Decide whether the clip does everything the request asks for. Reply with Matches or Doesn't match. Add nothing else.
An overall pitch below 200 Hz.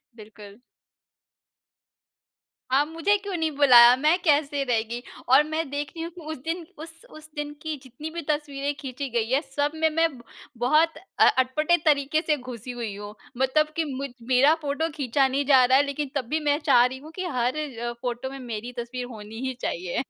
Doesn't match